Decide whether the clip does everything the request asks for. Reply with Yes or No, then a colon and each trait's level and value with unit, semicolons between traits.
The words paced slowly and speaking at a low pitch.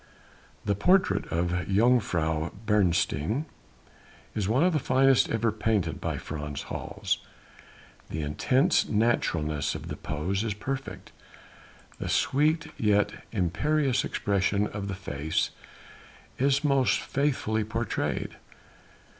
Yes: slow, 110 wpm; low, 105 Hz